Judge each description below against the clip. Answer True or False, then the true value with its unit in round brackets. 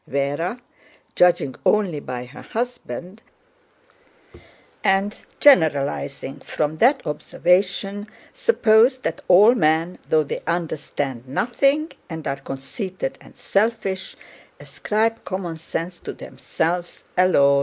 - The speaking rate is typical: False (100 wpm)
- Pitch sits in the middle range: True (180 Hz)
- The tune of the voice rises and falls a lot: True (6.6 semitones)